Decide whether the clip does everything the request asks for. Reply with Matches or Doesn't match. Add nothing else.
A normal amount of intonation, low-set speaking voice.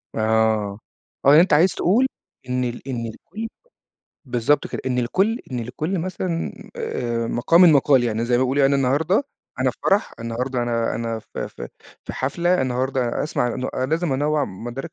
Matches